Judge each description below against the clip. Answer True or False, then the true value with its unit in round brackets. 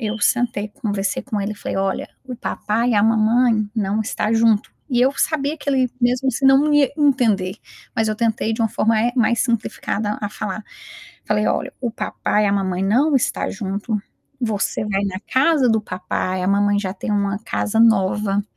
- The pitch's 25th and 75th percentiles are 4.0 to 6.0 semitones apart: False (3.2 semitones)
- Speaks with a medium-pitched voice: False (220 Hz)